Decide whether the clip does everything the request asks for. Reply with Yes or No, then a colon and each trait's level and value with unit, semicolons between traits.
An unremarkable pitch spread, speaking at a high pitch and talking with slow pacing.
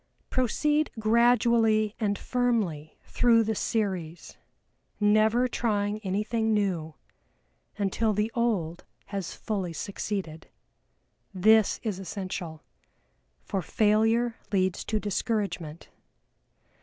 Yes: average, 3.1 semitones; high, 210 Hz; slow, 90 wpm